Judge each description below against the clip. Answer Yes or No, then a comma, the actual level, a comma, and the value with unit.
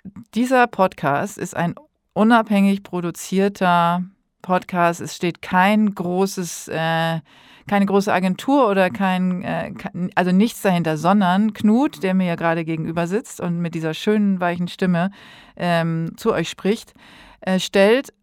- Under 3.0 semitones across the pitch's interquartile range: No, average, 3.3 semitones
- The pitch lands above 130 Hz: Yes, high, 190 Hz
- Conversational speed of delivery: No, slow, 120 wpm